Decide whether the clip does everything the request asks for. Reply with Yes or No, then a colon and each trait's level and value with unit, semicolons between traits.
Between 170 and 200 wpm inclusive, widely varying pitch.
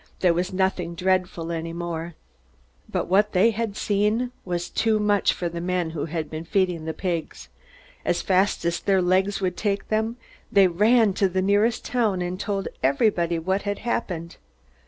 No: average, 175 wpm; average, 3.1 semitones